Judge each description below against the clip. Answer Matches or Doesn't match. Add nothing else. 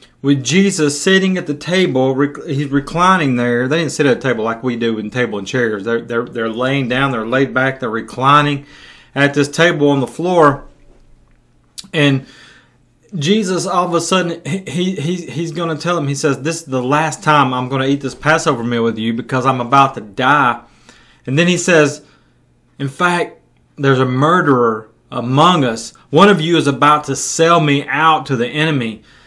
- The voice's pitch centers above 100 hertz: Matches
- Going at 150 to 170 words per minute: Doesn't match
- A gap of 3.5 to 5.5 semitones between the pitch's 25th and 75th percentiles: Matches